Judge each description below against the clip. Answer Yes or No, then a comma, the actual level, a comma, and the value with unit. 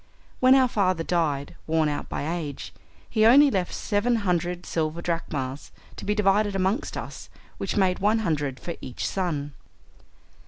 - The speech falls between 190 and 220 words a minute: No, average, 155 wpm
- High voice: No, medium, 180 Hz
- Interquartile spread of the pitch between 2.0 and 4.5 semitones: No, average, 4.9 semitones